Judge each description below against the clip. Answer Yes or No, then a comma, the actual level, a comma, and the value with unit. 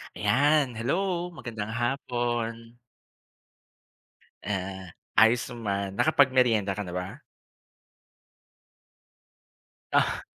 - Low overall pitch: Yes, low, 115 Hz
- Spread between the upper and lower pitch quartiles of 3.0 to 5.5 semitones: Yes, average, 4.0 semitones